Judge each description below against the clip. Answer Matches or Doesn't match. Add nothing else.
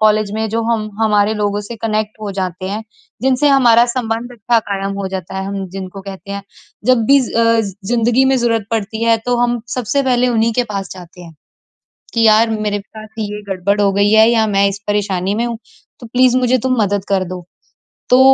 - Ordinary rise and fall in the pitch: Matches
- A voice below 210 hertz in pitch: Doesn't match